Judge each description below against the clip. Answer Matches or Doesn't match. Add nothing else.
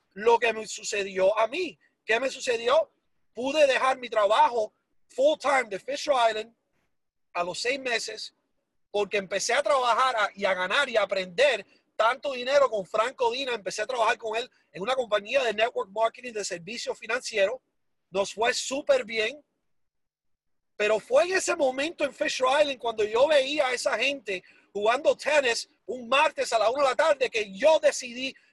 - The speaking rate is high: Doesn't match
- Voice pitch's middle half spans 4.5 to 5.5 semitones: Matches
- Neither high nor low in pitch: Doesn't match